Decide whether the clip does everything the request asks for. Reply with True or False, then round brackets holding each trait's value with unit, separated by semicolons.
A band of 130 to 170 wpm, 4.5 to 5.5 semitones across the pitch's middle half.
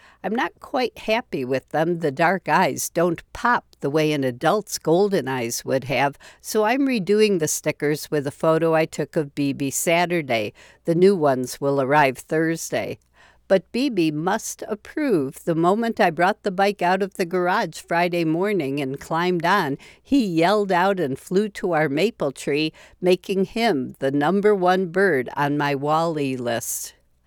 True (165 wpm; 5.1 semitones)